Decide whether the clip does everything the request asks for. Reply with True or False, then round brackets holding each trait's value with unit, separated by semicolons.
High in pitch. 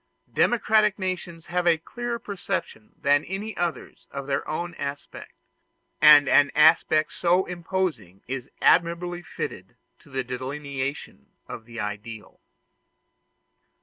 False (155 Hz)